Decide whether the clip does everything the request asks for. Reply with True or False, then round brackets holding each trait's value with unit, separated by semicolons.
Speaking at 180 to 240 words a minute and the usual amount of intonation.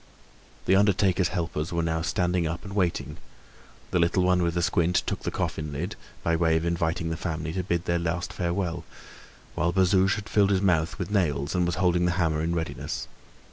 False (200 wpm; 1.9 semitones)